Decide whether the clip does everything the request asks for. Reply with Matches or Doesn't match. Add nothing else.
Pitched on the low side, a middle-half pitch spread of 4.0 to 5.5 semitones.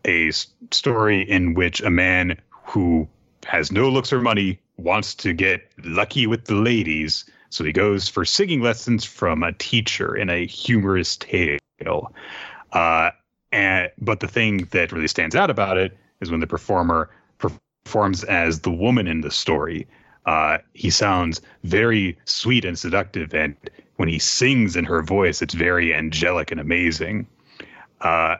Matches